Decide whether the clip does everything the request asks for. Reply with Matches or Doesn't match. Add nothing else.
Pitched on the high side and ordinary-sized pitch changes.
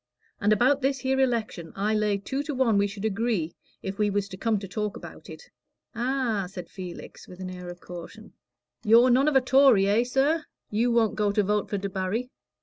Matches